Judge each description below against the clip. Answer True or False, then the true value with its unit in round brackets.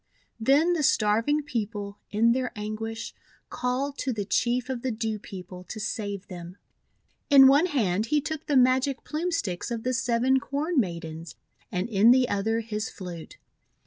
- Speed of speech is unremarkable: True (165 wpm)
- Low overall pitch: False (230 Hz)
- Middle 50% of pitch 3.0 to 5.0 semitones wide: True (4.5 semitones)